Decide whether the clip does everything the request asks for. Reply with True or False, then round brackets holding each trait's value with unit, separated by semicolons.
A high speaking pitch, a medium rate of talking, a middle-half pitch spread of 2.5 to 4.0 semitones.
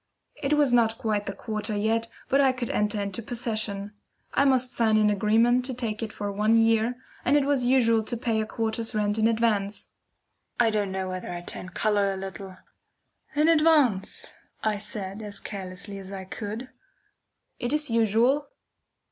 True (220 Hz; 175 wpm; 2.9 semitones)